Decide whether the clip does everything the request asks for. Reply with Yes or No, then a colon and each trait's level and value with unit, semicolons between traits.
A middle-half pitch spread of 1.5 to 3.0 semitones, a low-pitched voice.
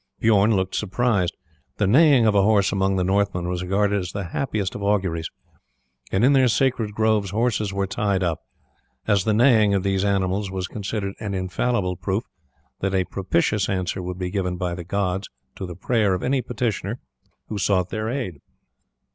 Yes: average, 2.7 semitones; low, 100 Hz